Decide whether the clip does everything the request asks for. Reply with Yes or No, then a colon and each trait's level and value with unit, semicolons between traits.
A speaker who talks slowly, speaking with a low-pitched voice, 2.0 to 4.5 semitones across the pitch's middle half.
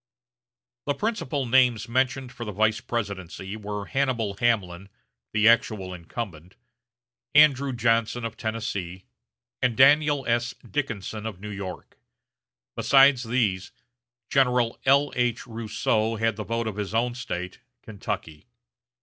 Yes: slow, 120 wpm; low, 115 Hz; average, 3.5 semitones